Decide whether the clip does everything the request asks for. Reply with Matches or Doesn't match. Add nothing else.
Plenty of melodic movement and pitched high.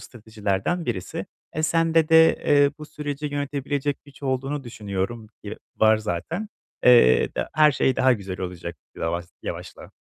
Doesn't match